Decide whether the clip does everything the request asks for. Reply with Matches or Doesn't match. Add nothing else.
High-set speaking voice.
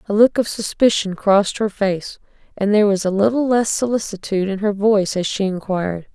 Matches